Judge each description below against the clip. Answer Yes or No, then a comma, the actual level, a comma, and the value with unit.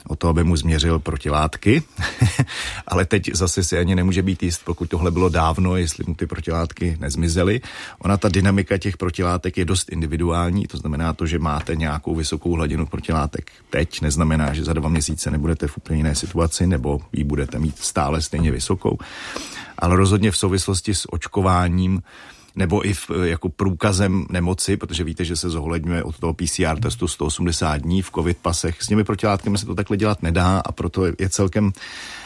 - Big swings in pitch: No, average, 2.8 semitones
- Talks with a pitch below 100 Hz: Yes, very low, 85 Hz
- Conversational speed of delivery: No, fast, 175 wpm